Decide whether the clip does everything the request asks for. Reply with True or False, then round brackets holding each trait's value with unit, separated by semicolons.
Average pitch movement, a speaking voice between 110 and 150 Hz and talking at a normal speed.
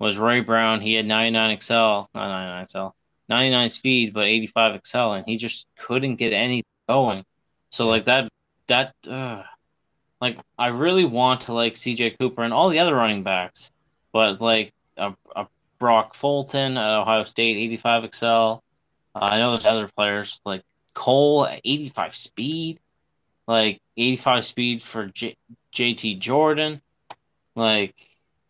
False (2.3 semitones; 115 Hz; 150 wpm)